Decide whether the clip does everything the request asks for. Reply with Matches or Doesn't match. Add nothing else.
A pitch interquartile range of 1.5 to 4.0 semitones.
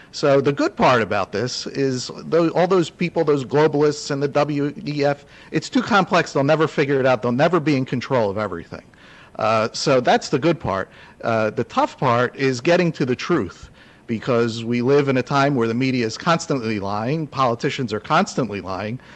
Doesn't match